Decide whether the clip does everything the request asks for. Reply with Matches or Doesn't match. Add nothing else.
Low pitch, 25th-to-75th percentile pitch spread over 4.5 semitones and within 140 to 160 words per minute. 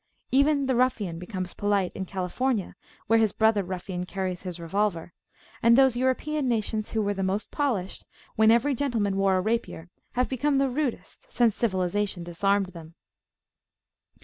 Doesn't match